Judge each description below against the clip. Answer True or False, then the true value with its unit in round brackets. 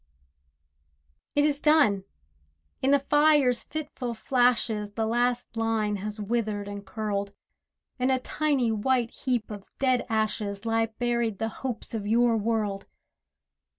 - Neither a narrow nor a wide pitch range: True (3.2 semitones)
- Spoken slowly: True (130 wpm)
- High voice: True (225 Hz)